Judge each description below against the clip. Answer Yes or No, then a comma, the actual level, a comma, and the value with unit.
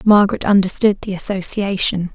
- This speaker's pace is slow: Yes, slow, 110 wpm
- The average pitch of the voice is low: No, high, 195 Hz